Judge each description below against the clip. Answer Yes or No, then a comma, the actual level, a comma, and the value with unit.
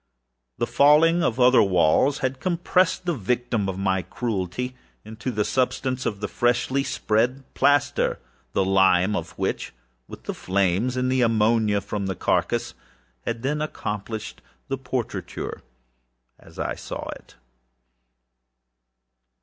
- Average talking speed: No, slow, 130 wpm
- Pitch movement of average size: Yes, average, 4.7 semitones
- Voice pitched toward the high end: No, low, 120 Hz